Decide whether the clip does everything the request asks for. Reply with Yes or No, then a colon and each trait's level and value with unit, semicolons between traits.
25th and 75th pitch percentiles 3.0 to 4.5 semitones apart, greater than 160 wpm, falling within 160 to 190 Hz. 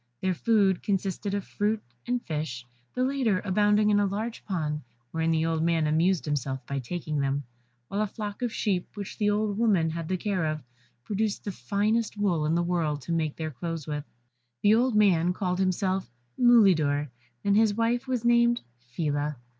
No: average, 5.1 semitones; average, 185 wpm; medium, 185 Hz